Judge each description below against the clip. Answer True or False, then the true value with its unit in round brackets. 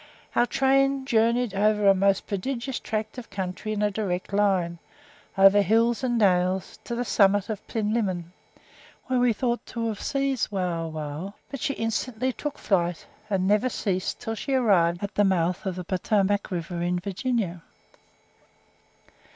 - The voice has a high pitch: True (205 Hz)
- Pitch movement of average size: True (4.3 semitones)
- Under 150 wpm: False (155 wpm)